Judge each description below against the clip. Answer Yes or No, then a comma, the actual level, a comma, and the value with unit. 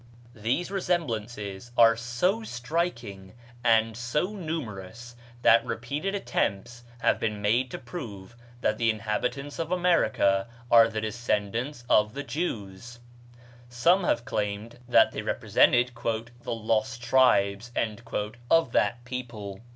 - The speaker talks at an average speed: No, slow, 120 wpm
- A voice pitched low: Yes, low, 120 Hz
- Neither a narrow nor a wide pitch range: Yes, average, 3.5 semitones